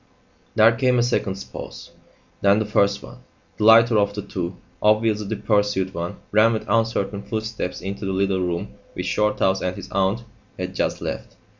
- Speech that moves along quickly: No, average, 175 wpm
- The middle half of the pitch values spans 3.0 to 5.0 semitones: No, narrow, 2.4 semitones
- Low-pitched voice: Yes, low, 105 Hz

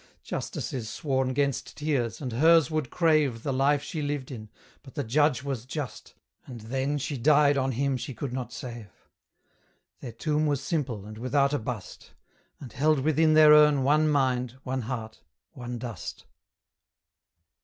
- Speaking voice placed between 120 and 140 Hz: Yes, low, 135 Hz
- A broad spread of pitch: No, average, 3.2 semitones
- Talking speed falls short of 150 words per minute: No, average, 165 wpm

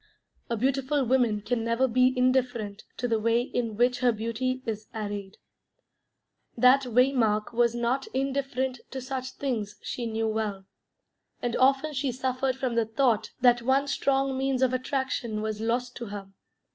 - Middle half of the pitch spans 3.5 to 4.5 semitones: No, average, 2.7 semitones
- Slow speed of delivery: No, average, 160 wpm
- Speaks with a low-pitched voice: No, high, 245 Hz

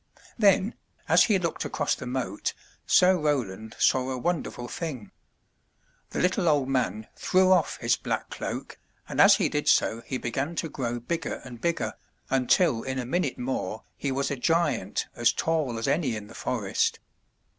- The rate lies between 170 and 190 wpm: Yes, average, 175 wpm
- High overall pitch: No, low, 130 Hz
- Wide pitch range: Yes, wide, 5.8 semitones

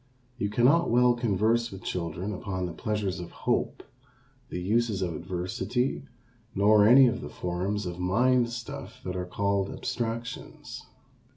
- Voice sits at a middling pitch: No, low, 105 Hz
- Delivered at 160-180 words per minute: No, average, 145 wpm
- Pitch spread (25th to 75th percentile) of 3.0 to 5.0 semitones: Yes, average, 4.5 semitones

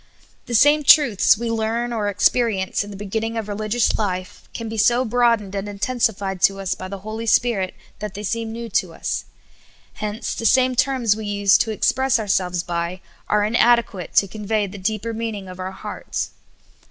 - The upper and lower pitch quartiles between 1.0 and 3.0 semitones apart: Yes, average, 2.7 semitones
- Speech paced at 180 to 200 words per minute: Yes, average, 190 wpm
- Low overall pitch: No, high, 215 Hz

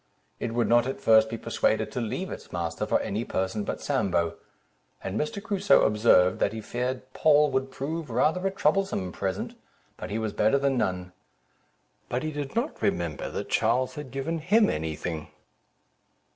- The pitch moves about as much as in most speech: No, wide, 6.6 semitones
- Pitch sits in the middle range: No, low, 125 Hz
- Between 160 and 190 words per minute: Yes, average, 175 wpm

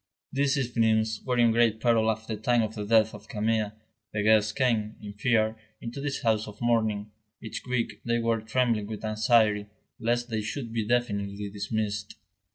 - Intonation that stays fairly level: Yes, narrow, 1.8 semitones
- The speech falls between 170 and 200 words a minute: Yes, average, 175 wpm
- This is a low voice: Yes, low, 110 Hz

